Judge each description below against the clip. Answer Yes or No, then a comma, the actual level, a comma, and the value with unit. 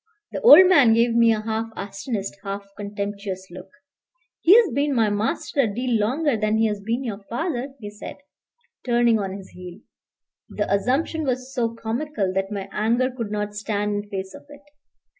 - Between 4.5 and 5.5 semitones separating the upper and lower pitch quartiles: No, average, 3.8 semitones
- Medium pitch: No, high, 220 Hz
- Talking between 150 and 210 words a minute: Yes, average, 175 wpm